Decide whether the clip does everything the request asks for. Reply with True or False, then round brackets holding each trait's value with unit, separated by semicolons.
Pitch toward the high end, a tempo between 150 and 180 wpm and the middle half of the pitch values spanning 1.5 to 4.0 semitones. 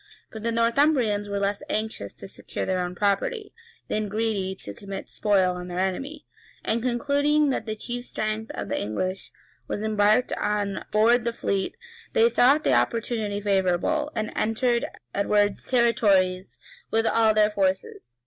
True (215 Hz; 155 wpm; 3.4 semitones)